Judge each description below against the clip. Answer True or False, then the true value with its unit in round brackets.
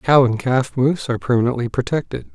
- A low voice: True (125 Hz)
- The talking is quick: False (180 wpm)